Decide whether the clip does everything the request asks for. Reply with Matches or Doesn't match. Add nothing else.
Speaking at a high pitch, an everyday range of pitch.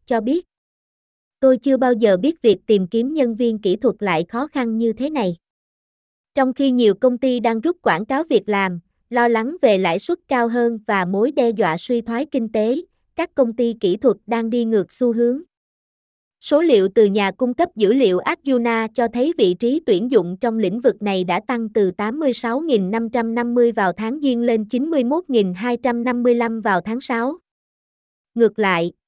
Matches